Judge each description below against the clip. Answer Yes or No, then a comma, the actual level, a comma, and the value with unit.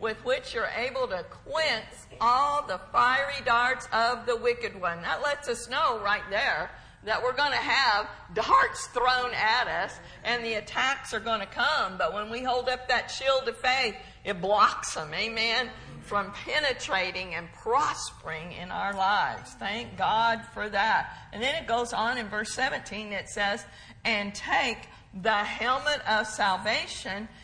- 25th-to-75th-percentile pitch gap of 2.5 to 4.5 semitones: Yes, average, 3.9 semitones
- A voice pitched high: Yes, high, 235 Hz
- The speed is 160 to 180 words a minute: Yes, average, 165 wpm